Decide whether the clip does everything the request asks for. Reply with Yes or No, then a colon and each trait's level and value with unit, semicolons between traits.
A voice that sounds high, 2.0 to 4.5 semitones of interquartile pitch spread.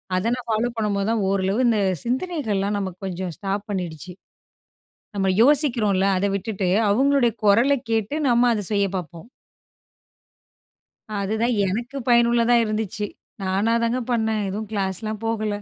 Yes: high, 215 Hz; average, 3.2 semitones